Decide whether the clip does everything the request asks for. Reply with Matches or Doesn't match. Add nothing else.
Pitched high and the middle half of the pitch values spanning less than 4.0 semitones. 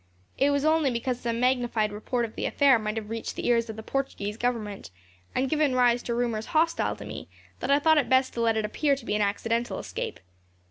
Matches